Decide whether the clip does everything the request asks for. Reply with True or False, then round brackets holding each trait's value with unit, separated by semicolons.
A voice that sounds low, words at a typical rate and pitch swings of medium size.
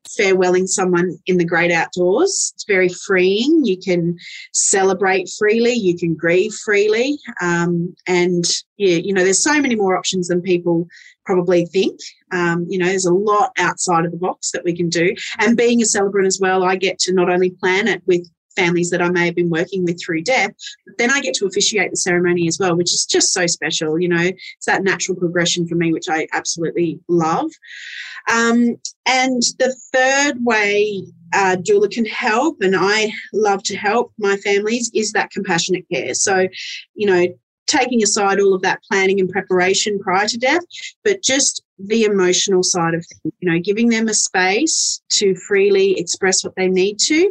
False (190 Hz; 190 wpm; 3.5 semitones)